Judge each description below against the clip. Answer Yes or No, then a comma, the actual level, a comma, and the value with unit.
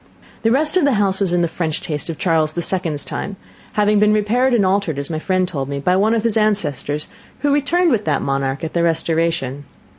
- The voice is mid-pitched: Yes, medium, 180 Hz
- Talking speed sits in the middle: No, fast, 230 wpm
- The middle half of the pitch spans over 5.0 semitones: Yes, wide, 5.4 semitones